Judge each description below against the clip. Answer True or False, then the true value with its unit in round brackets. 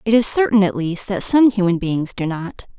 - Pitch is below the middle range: False (200 Hz)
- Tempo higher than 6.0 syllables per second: False (5.1 syllables/s)